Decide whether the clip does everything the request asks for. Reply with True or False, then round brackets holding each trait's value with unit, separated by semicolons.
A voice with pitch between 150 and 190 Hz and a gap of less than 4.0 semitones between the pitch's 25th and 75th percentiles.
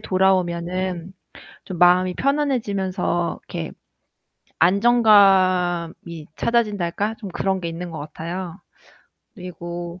True (185 Hz; 2.6 semitones)